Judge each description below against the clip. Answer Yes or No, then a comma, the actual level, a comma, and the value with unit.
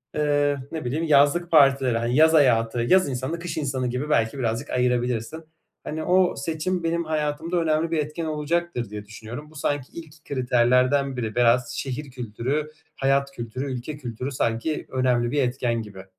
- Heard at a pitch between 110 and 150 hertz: Yes, medium, 140 Hz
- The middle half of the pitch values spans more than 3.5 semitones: Yes, average, 4.0 semitones